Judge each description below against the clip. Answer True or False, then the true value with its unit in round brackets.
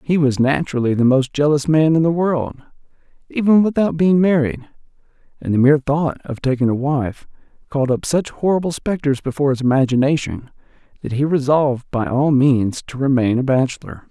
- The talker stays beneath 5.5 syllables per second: False (5.6 syllables/s)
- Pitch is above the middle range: False (140 Hz)